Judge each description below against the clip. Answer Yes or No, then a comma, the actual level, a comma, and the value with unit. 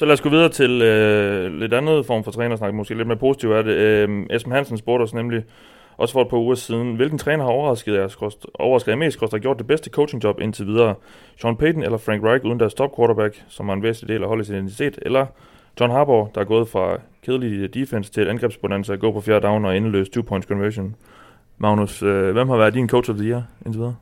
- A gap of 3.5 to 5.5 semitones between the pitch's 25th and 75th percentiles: No, average, 2.8 semitones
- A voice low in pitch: Yes, low, 115 Hz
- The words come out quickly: Yes, fast, 230 wpm